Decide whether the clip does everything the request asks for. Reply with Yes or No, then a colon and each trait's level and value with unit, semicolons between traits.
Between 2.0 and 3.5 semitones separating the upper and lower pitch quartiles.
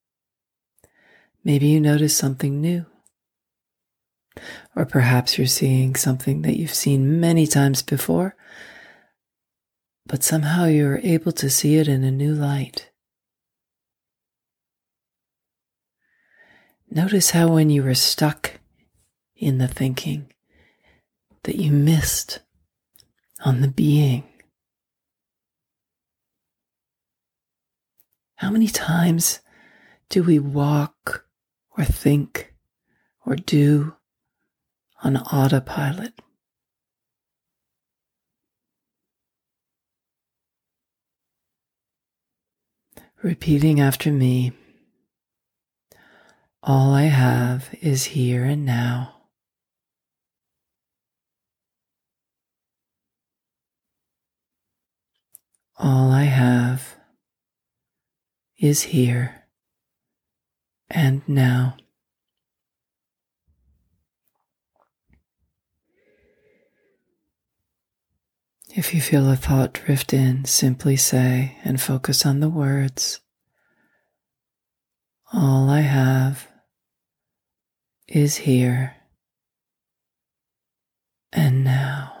Yes: average, 2.9 semitones